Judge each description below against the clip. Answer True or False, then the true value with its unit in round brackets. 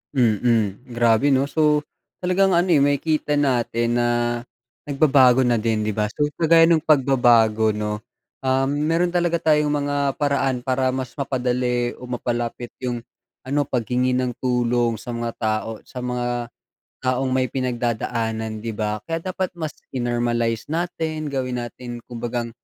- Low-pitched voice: True (125 Hz)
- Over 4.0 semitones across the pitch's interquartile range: False (3.5 semitones)